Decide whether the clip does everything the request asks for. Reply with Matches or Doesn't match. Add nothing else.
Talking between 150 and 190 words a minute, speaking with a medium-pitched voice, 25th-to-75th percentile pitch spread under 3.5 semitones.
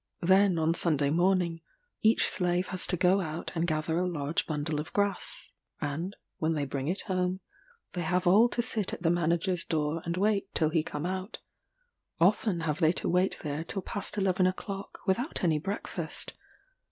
Matches